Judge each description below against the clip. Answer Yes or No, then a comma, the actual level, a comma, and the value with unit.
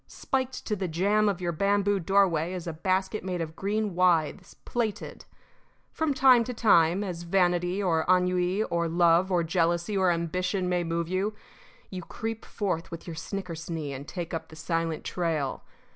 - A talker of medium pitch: Yes, medium, 180 Hz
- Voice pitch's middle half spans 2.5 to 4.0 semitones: Yes, average, 3.0 semitones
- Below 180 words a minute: Yes, average, 170 wpm